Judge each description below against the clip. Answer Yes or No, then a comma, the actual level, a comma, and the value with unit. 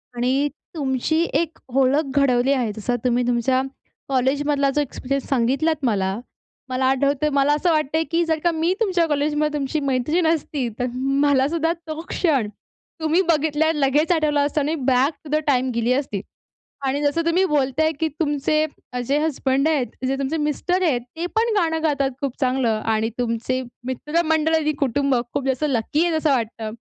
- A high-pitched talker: Yes, very high, 285 Hz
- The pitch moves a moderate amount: Yes, average, 3.4 semitones